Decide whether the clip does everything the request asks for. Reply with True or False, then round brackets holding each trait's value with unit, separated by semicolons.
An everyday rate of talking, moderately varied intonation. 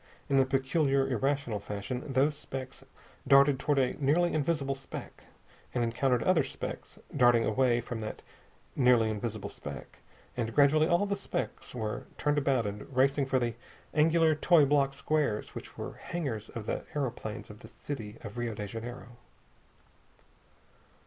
True (155 wpm; 3.7 semitones)